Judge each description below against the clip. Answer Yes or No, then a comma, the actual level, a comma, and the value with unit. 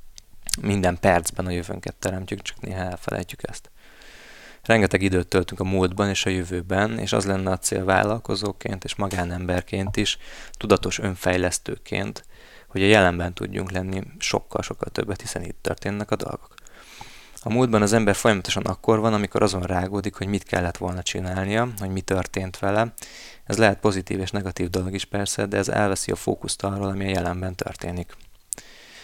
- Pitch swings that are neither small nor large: No, narrow, 2.2 semitones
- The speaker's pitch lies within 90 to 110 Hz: Yes, very low, 95 Hz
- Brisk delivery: Yes, fast, 160 wpm